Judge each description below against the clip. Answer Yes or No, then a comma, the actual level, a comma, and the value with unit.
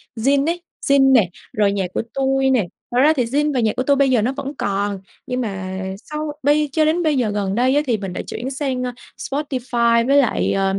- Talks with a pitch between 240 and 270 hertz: Yes, very high, 255 Hz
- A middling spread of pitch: Yes, average, 4.6 semitones